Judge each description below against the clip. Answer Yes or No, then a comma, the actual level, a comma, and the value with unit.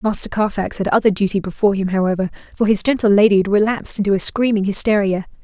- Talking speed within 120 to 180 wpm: No, average, 200 wpm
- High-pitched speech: Yes, high, 200 Hz